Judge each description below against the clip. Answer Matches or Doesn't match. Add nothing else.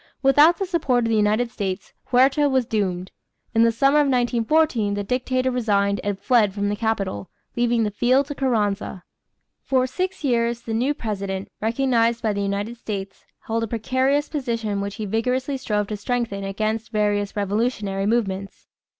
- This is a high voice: Matches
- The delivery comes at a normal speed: Matches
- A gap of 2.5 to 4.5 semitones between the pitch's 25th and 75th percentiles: Matches